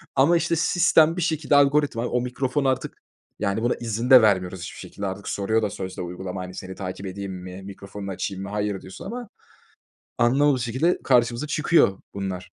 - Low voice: Yes, low, 110 Hz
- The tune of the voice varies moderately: No, wide, 6.3 semitones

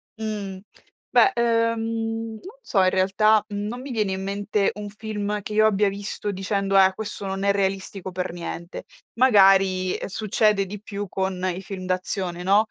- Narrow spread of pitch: Yes, narrow, 1.9 semitones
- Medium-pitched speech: No, high, 200 Hz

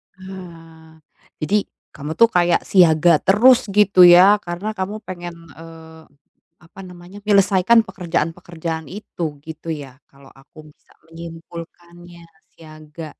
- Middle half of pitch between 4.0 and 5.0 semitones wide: No, average, 2.9 semitones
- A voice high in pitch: No, medium, 175 Hz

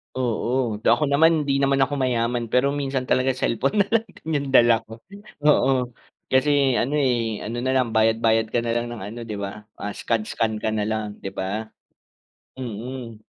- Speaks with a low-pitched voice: Yes, low, 120 Hz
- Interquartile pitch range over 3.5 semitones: No, average, 3.2 semitones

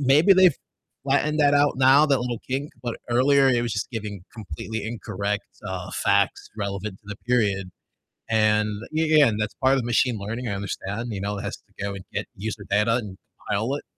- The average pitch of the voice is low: Yes, low, 110 Hz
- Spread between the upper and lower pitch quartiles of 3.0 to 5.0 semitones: Yes, average, 4.6 semitones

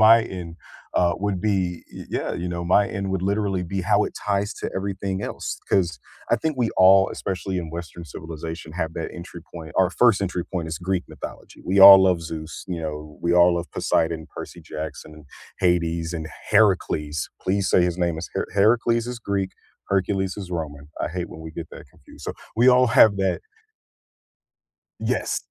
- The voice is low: Yes, very low, 90 Hz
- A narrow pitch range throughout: No, average, 3.0 semitones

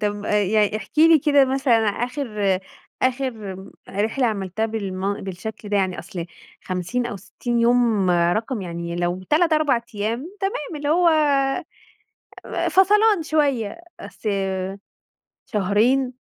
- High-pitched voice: Yes, high, 225 Hz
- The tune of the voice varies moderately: No, wide, 5.8 semitones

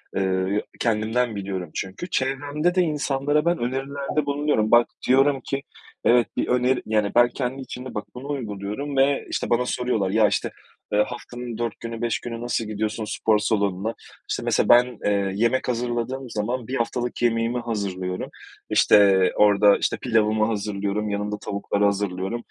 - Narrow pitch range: No, average, 3.7 semitones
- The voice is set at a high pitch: No, low, 115 Hz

